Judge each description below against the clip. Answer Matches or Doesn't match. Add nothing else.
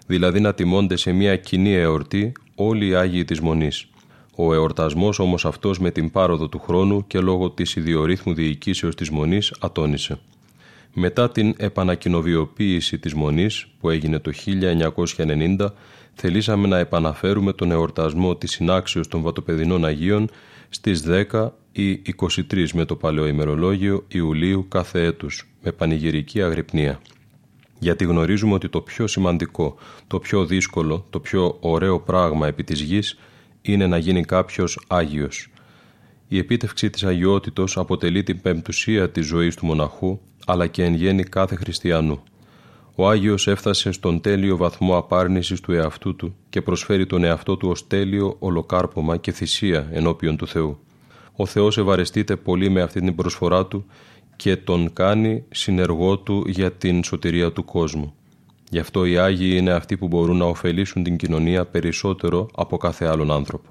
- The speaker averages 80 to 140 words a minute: Doesn't match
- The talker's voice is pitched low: Matches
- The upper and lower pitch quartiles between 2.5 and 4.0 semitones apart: Matches